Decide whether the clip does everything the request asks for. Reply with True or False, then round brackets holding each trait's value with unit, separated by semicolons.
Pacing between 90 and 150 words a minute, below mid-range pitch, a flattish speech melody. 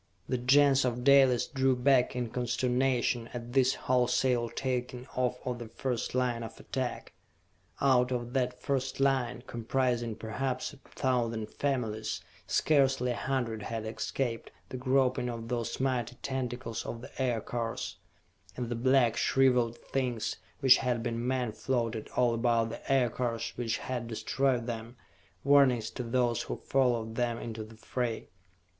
True (145 wpm; 125 Hz; 1.9 semitones)